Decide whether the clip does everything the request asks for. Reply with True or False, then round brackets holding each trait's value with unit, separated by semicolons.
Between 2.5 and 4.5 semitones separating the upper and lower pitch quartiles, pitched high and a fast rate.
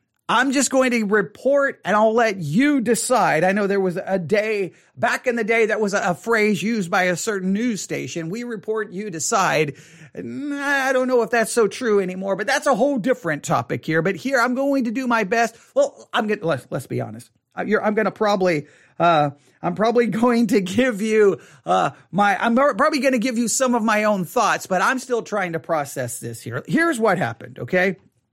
False (5.0 semitones; 215 Hz; 220 wpm)